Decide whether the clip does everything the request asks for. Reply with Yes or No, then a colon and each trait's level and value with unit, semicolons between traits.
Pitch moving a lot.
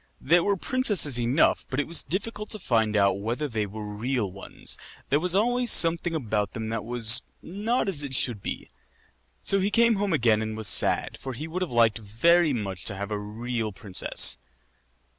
Yes: wide, 8.3 semitones